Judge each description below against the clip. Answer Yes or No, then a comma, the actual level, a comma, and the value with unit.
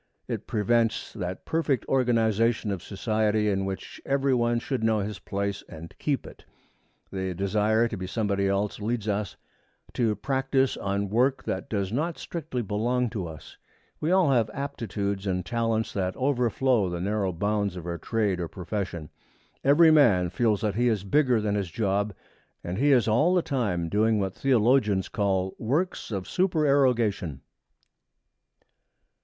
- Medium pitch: No, low, 110 Hz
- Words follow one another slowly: No, average, 155 wpm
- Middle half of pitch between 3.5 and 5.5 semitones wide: Yes, average, 4.2 semitones